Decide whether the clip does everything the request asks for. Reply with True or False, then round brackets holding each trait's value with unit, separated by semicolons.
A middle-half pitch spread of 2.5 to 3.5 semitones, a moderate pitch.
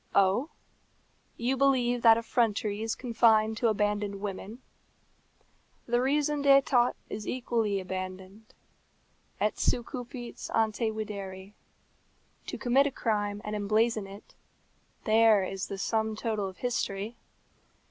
False (2.9 semitones; 220 Hz)